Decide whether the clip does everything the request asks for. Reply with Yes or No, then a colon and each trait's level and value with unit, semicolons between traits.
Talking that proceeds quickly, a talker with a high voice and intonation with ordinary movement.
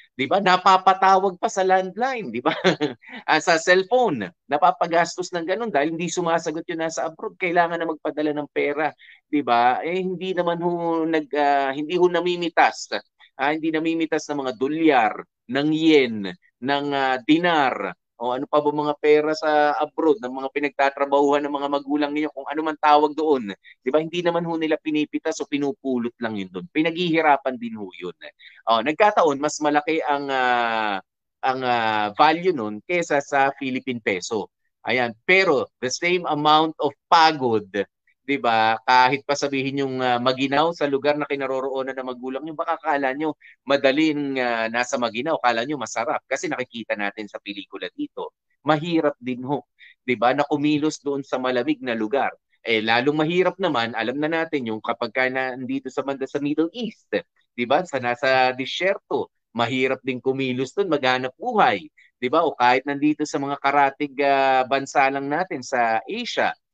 No: fast, 165 wpm; medium, 145 Hz; average, 3.8 semitones